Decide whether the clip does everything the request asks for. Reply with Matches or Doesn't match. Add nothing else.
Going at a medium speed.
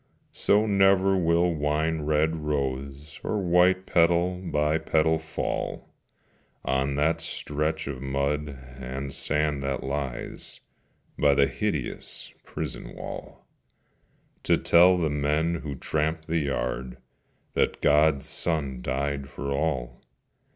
Doesn't match